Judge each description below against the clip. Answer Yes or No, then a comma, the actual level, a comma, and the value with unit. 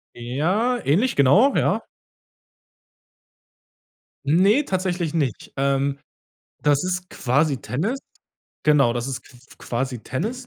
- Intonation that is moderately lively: No, wide, 5.9 semitones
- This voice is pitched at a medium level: Yes, medium, 150 Hz